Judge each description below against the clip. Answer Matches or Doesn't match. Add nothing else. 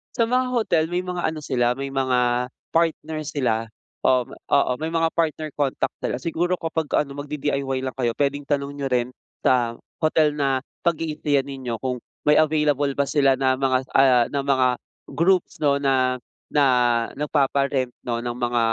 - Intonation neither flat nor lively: Matches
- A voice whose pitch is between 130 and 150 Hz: Matches